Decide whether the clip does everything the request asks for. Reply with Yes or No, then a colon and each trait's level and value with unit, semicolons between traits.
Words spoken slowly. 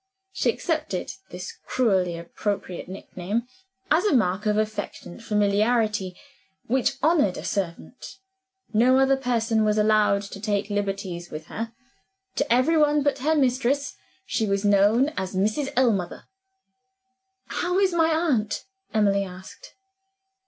Yes: slow, 130 wpm